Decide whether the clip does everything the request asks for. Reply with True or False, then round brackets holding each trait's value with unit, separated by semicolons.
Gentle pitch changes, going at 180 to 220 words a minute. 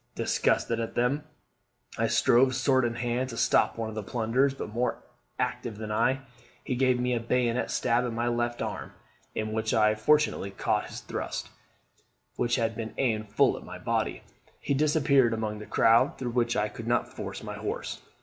True (2.3 semitones; 190 wpm)